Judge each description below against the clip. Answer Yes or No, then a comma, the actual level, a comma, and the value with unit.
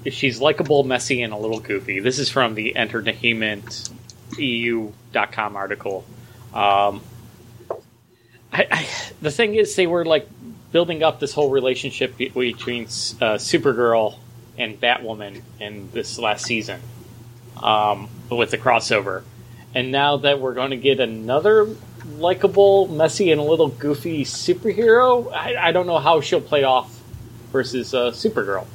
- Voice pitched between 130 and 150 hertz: No, low, 120 Hz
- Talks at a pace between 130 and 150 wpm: Yes, average, 140 wpm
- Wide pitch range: No, average, 4.3 semitones